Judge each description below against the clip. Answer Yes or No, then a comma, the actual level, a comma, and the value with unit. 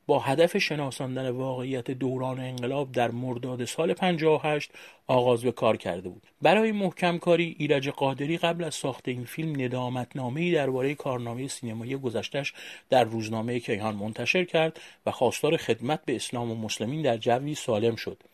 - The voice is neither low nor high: No, low, 130 Hz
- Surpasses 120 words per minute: Yes, fast, 155 wpm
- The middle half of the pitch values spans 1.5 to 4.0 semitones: Yes, average, 3.7 semitones